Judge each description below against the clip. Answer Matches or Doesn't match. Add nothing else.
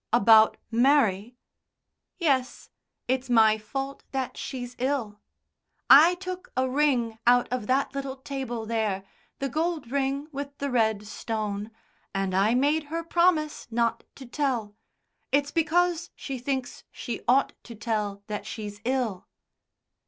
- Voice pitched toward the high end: Matches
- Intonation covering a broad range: Doesn't match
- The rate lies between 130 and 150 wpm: Matches